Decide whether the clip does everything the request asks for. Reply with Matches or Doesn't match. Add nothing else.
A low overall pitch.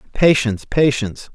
Matches